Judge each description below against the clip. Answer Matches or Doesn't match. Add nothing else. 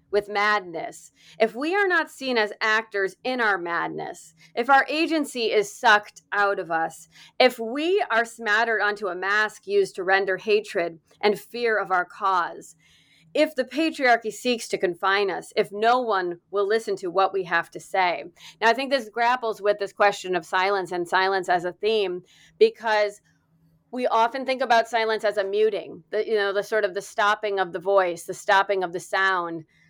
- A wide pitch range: Doesn't match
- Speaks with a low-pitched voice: Doesn't match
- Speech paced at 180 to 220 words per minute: Matches